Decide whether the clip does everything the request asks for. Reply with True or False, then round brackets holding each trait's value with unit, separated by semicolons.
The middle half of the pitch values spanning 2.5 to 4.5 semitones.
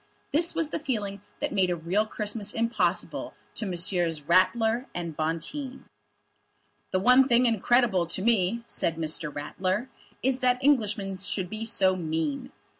False (5.2 semitones)